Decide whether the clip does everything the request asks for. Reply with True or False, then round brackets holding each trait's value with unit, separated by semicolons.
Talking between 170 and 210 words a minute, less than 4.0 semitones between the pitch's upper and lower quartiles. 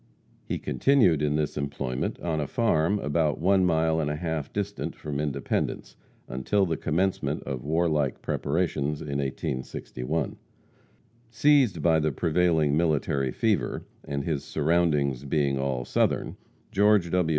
False (135 wpm; 3.4 semitones)